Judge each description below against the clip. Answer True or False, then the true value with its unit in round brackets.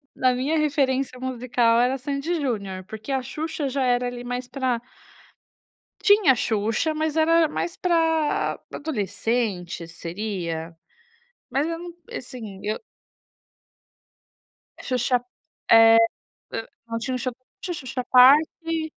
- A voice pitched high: True (255 Hz)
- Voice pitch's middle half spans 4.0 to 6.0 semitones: True (5.2 semitones)